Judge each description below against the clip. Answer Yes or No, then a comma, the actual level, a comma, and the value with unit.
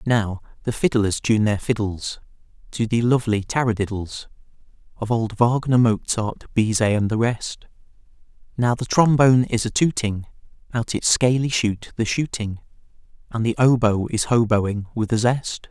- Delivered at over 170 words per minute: No, average, 145 wpm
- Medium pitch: No, low, 115 Hz